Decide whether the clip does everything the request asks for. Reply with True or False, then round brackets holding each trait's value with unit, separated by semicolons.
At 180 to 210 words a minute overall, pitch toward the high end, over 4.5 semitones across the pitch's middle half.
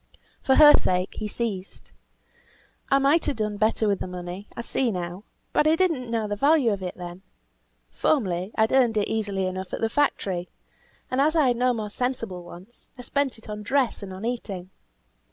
True (200 wpm; 220 Hz; 5.3 semitones)